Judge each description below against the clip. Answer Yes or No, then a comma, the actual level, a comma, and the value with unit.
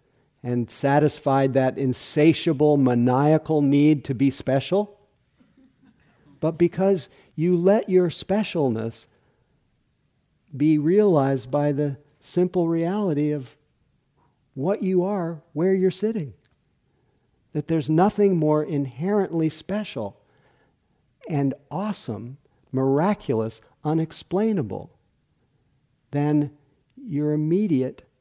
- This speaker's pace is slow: Yes, slow, 85 wpm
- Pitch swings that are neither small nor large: Yes, average, 4.6 semitones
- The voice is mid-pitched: Yes, medium, 150 Hz